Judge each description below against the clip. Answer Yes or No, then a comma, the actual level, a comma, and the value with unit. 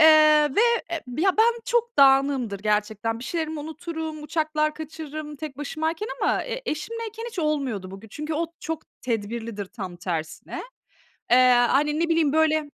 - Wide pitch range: No, average, 5.0 semitones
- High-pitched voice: Yes, very high, 300 Hz